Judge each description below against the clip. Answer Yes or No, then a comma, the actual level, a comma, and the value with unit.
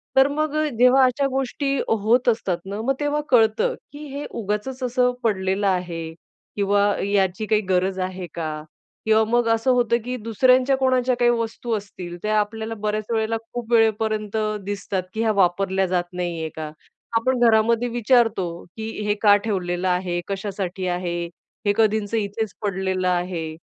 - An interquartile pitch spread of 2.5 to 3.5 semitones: No, average, 4.1 semitones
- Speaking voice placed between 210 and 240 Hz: Yes, high, 215 Hz